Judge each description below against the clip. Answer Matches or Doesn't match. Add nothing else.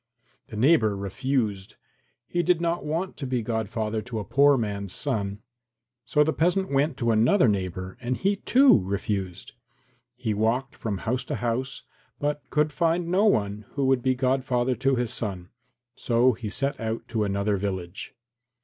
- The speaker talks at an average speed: Matches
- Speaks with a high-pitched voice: Doesn't match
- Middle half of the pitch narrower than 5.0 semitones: Doesn't match